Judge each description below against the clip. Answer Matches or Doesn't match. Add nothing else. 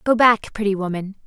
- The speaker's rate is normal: Matches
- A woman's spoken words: Matches